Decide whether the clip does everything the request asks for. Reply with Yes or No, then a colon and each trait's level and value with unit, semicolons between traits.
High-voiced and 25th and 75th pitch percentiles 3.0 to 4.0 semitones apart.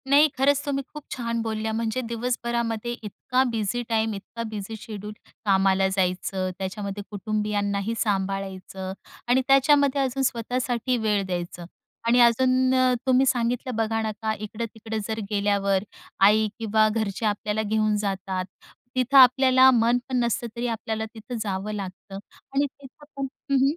Yes: high, 220 Hz; average, 3.7 semitones